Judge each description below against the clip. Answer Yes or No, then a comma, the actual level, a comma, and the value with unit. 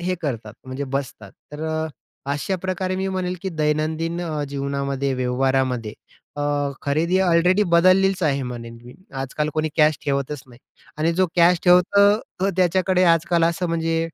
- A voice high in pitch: No, medium, 160 Hz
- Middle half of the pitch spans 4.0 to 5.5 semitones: Yes, average, 4.5 semitones